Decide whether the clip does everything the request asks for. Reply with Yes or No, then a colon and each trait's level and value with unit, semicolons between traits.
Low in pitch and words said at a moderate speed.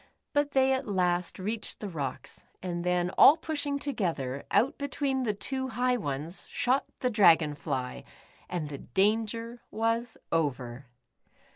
No: high, 205 Hz; average, 150 wpm